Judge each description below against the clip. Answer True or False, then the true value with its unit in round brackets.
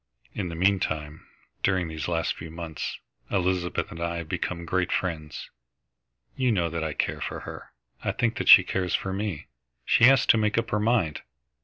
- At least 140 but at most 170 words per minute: False (185 wpm)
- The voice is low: True (90 Hz)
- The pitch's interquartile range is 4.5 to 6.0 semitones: False (3.7 semitones)